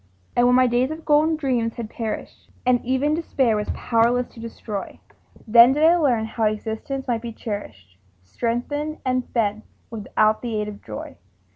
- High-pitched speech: Yes, high, 235 Hz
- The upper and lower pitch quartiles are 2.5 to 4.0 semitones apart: Yes, average, 3.2 semitones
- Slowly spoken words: No, average, 170 wpm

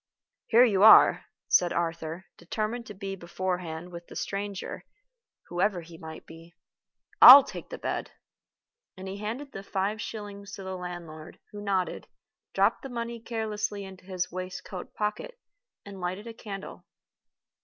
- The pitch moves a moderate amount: Yes, average, 3.1 semitones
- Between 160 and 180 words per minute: No, average, 145 wpm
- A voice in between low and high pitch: No, high, 195 Hz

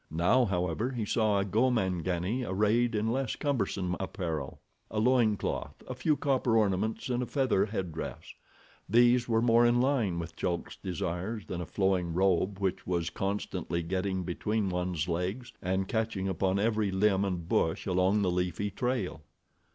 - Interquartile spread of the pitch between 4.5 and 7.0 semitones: No, average, 4.1 semitones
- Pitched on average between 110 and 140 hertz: No, low, 100 Hz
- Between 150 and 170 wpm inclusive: Yes, average, 155 wpm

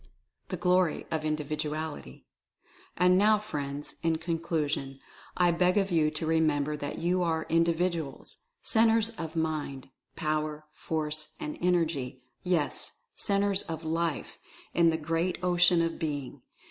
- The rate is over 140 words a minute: No, slow, 135 wpm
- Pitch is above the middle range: No, medium, 160 Hz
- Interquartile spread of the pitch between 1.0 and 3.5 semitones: Yes, average, 2.7 semitones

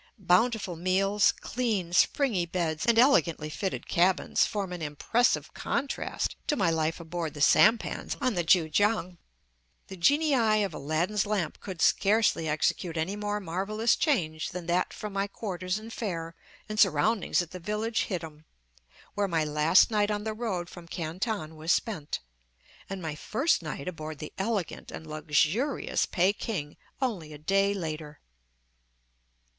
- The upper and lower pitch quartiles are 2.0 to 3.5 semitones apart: No, average, 4.7 semitones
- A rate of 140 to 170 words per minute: Yes, average, 150 wpm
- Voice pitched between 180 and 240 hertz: Yes, medium, 185 Hz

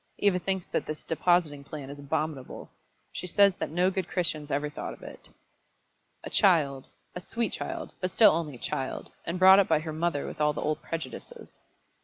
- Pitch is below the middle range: No, medium, 160 Hz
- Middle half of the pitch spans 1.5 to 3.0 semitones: No, average, 3.7 semitones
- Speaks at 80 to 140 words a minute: No, average, 195 wpm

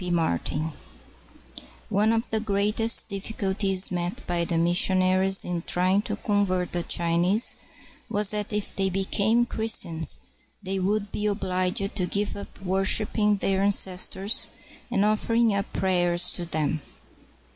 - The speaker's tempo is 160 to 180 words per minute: No, average, 140 wpm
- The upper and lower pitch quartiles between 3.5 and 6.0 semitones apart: No, narrow, 2.6 semitones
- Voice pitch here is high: Yes, high, 195 Hz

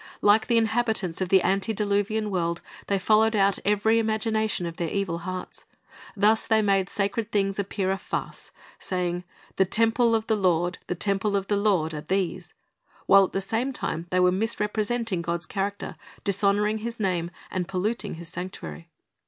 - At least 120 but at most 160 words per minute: No, average, 170 wpm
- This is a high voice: Yes, high, 200 Hz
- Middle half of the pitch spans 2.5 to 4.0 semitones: Yes, average, 3.1 semitones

